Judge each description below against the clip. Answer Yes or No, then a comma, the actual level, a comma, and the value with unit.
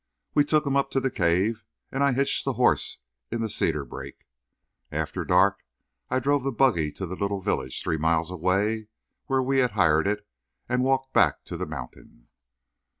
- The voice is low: Yes, low, 105 Hz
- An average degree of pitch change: No, wide, 7.8 semitones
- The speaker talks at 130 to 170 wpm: No, average, 185 wpm